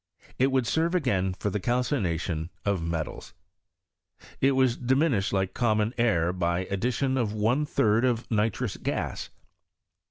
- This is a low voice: Yes, low, 110 Hz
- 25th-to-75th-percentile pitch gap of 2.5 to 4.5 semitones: No, average, 5.2 semitones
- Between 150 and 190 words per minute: No, slow, 135 wpm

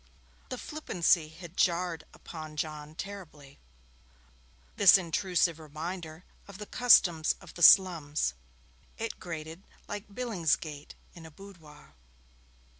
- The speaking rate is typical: No, slow, 110 wpm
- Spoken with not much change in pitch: No, average, 3.4 semitones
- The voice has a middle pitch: Yes, medium, 170 Hz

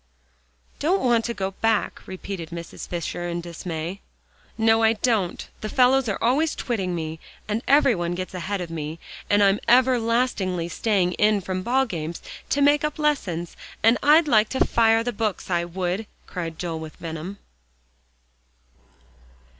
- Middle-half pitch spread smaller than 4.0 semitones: No, average, 5.3 semitones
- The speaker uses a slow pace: No, average, 155 wpm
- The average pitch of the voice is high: Yes, high, 200 Hz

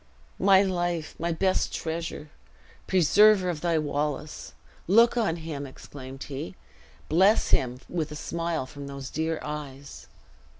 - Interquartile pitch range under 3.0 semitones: No, average, 3.6 semitones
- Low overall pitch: No, medium, 160 Hz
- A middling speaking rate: No, slow, 130 wpm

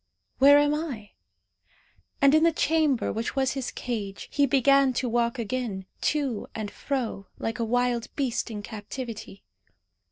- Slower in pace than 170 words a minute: Yes, average, 150 wpm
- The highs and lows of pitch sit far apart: No, average, 3.7 semitones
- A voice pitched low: No, very high, 250 Hz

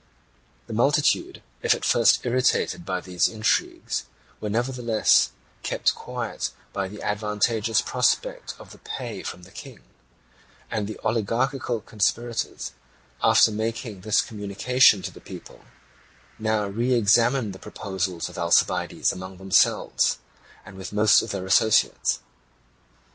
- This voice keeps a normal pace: No, slow, 125 wpm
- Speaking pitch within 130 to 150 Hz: No, low, 110 Hz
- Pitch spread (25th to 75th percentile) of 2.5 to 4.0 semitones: Yes, average, 3.3 semitones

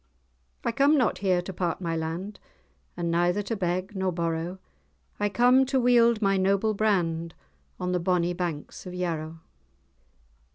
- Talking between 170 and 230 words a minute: No, average, 155 wpm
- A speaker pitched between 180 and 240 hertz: Yes, medium, 185 Hz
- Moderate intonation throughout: Yes, average, 3.5 semitones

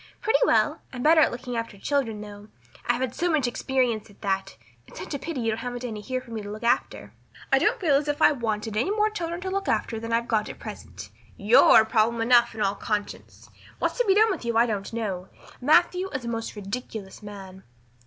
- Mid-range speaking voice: No, high, 235 Hz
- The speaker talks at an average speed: No, fast, 225 wpm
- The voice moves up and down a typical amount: Yes, average, 5.0 semitones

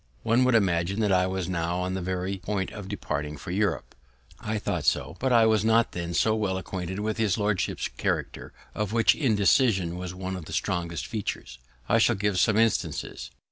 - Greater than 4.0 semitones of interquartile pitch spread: No, average, 3.3 semitones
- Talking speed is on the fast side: No, average, 195 wpm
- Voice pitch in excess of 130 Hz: No, very low, 95 Hz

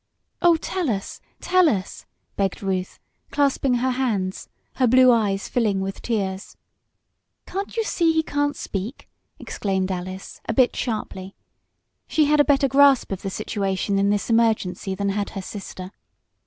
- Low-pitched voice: No, high, 215 Hz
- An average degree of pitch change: No, wide, 5.9 semitones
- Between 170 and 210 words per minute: No, average, 155 wpm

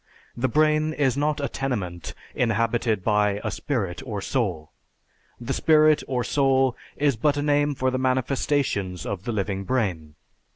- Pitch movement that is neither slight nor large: No, wide, 5.7 semitones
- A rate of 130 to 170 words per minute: Yes, average, 155 wpm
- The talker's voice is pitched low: Yes, low, 125 Hz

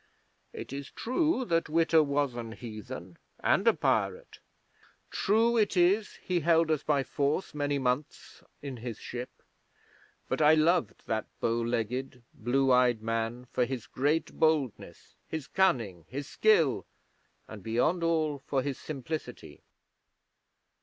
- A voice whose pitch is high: No, medium, 140 Hz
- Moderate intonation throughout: Yes, average, 5.0 semitones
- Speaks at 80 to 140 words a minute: Yes, slow, 135 wpm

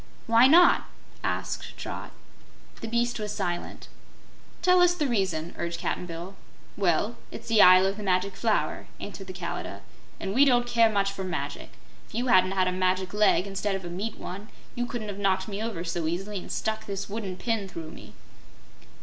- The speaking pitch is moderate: No, high, 195 Hz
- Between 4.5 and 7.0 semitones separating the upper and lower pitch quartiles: No, average, 3.6 semitones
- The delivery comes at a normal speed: Yes, average, 190 wpm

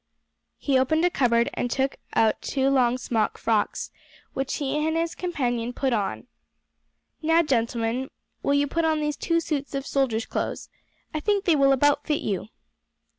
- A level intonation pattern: No, average, 4.1 semitones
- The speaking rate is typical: Yes, average, 170 wpm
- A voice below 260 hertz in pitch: No, very high, 275 Hz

